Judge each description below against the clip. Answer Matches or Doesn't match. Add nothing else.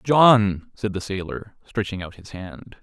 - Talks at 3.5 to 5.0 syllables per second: Matches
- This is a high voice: Doesn't match